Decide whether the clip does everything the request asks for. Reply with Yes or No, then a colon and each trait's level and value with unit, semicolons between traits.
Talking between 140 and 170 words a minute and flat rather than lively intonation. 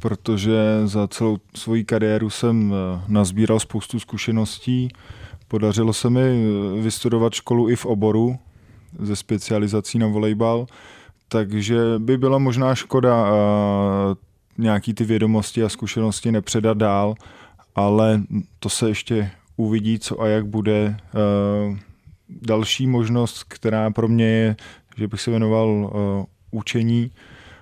No: slow, 115 wpm; narrow, 1.8 semitones